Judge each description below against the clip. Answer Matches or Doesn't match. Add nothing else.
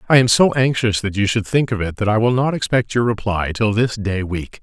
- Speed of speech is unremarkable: Doesn't match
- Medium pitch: Doesn't match